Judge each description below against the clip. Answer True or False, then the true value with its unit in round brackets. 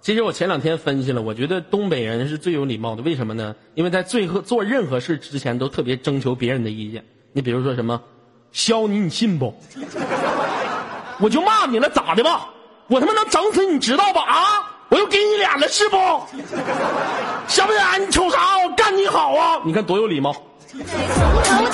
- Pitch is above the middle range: True (200 Hz)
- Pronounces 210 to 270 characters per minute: False (280 characters per minute)